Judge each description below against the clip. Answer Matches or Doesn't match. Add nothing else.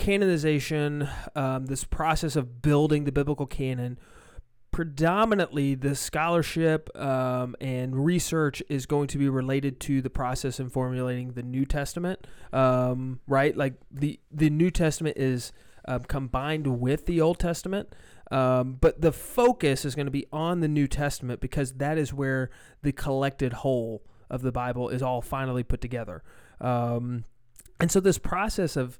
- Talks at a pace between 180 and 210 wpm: Doesn't match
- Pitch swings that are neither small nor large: Matches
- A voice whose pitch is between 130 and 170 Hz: Matches